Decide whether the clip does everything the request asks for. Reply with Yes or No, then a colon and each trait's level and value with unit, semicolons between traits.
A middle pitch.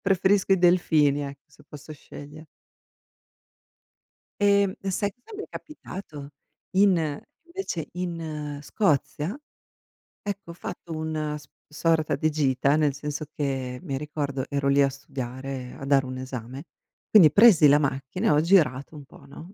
Yes: medium, 150 Hz